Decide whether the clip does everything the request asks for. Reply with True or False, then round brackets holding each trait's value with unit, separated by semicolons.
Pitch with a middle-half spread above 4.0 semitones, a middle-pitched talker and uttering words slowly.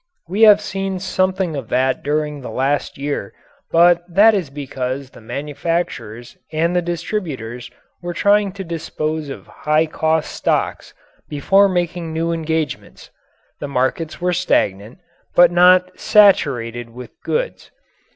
True (4.7 semitones; 160 Hz; 130 wpm)